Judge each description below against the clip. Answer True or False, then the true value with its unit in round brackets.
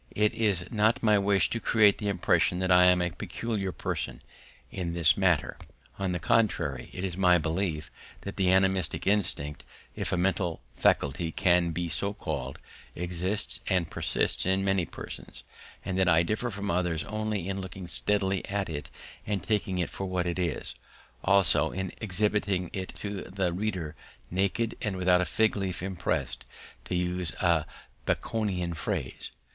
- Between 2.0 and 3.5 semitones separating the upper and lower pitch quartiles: True (2.4 semitones)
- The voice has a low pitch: True (95 Hz)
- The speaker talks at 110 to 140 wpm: False (165 wpm)